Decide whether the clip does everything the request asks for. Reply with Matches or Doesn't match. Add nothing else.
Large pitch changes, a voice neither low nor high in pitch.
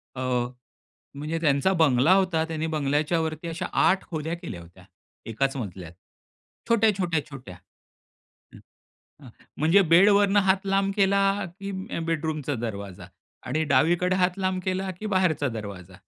Matches